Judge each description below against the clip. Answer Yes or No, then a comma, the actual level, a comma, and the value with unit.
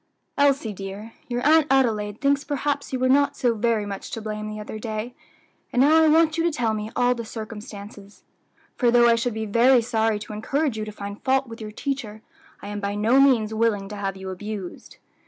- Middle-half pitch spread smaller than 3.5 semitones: No, average, 4.0 semitones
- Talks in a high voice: Yes, high, 225 Hz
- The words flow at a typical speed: No, fast, 215 wpm